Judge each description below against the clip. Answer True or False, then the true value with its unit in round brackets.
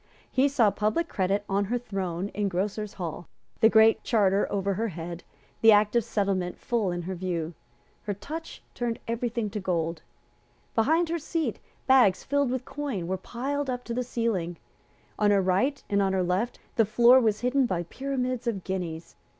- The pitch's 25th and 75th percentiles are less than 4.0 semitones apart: False (4.7 semitones)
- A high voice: True (210 Hz)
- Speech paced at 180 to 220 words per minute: True (185 wpm)